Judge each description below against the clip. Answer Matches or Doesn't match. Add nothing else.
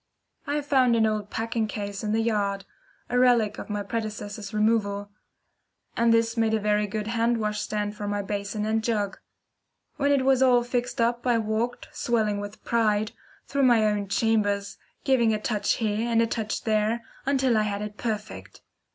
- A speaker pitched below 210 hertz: Doesn't match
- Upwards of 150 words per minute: Matches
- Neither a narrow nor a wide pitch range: Doesn't match